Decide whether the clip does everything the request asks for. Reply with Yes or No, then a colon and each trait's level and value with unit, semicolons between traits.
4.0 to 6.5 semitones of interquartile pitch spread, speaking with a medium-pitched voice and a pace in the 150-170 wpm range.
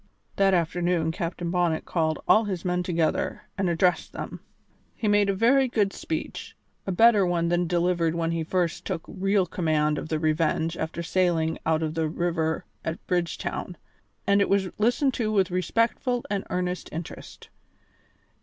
No: average, 3.2 semitones; medium, 175 Hz; average, 165 wpm